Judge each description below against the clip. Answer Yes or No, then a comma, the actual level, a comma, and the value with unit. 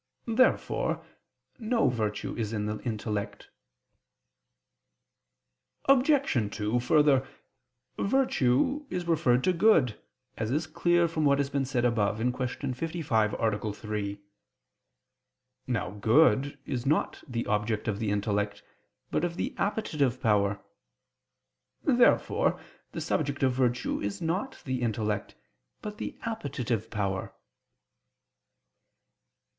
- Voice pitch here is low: Yes, low, 125 Hz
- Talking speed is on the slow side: Yes, slow, 110 wpm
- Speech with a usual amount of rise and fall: No, wide, 7.1 semitones